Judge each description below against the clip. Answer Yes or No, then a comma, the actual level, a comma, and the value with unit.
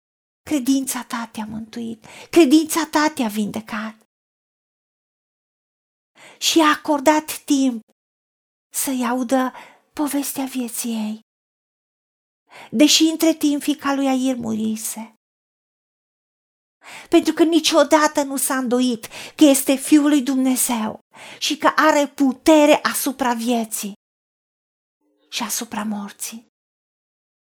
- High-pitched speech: Yes, very high, 265 Hz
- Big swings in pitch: No, average, 4.4 semitones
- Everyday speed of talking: No, slow, 95 wpm